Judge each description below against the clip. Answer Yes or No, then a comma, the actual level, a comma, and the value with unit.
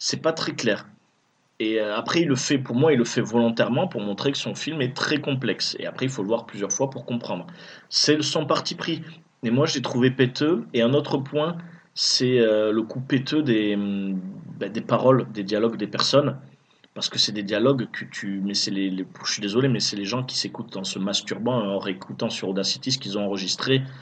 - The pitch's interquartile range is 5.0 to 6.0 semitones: Yes, wide, 5.5 semitones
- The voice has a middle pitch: No, low, 120 Hz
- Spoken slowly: No, fast, 220 wpm